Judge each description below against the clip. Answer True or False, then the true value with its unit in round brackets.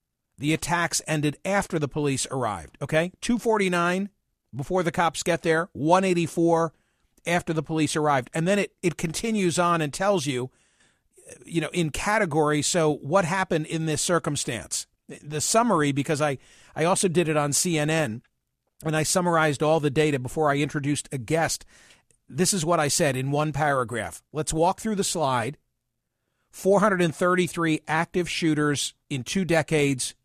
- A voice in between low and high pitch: True (160 Hz)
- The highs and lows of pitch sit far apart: False (3.2 semitones)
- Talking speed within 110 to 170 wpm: True (155 wpm)